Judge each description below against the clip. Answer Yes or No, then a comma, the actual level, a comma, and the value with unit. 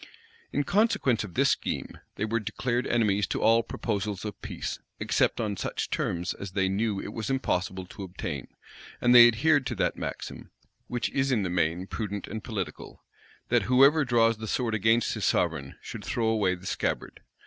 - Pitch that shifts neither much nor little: Yes, average, 3.7 semitones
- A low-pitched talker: Yes, low, 110 Hz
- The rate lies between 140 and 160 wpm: No, average, 180 wpm